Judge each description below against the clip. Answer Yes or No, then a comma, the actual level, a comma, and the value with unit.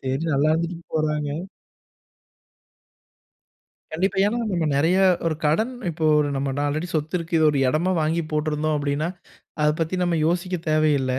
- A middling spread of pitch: No, narrow, 2.3 semitones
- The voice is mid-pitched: Yes, medium, 155 Hz